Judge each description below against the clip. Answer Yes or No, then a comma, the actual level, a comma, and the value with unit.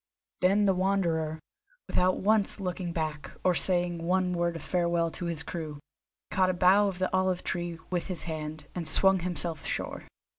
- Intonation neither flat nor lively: No, narrow, 2.1 semitones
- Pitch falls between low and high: Yes, medium, 175 Hz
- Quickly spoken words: No, average, 175 wpm